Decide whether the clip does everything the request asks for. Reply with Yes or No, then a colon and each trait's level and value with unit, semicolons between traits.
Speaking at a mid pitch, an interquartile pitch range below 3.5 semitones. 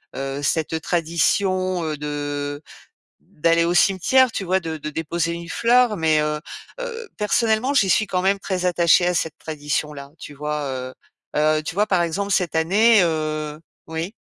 No: medium, 165 Hz; average, 4.2 semitones